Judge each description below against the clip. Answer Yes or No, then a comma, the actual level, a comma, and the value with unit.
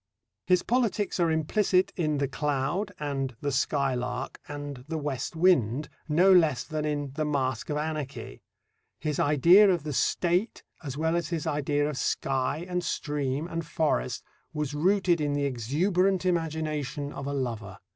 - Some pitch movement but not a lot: Yes, average, 3.7 semitones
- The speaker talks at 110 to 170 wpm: Yes, average, 155 wpm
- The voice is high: No, medium, 150 Hz